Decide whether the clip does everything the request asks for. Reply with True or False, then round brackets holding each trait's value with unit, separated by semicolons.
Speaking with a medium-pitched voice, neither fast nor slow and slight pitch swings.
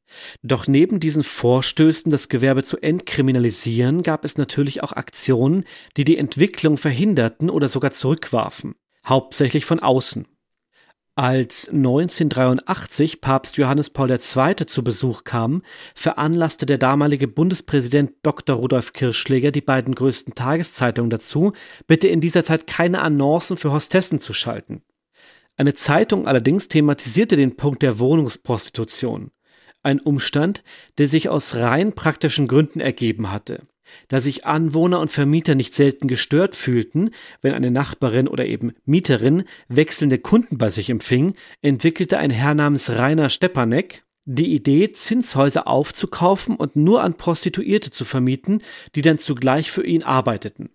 False (145 Hz; 135 wpm; 3.6 semitones)